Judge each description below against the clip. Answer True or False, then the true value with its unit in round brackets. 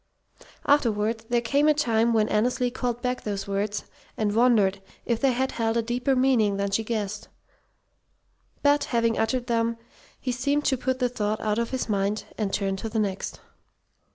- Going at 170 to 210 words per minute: True (180 wpm)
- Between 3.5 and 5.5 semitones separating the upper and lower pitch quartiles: False (2.9 semitones)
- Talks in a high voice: True (230 Hz)